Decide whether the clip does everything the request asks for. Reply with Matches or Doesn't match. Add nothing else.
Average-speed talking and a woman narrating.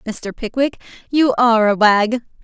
Matches